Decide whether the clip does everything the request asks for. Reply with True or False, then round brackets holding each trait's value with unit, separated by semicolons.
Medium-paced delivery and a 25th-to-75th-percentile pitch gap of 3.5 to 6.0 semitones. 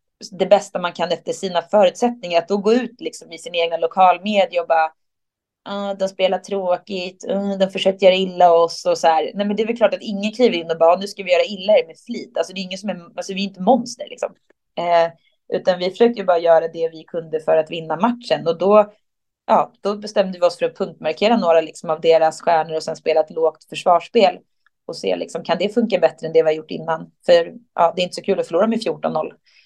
False (250 wpm; 3.8 semitones)